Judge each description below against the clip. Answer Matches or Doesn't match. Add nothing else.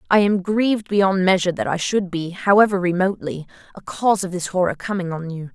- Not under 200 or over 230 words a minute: Matches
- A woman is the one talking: Matches